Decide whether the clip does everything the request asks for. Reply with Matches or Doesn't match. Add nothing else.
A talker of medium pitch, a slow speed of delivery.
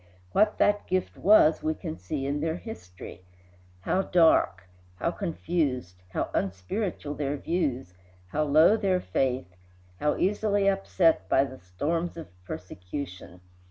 Matches